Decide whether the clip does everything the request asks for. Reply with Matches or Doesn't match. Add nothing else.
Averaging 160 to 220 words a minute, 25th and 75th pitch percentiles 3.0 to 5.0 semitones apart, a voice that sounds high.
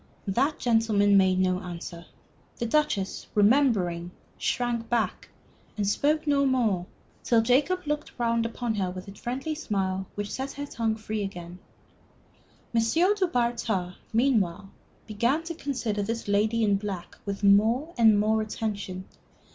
Doesn't match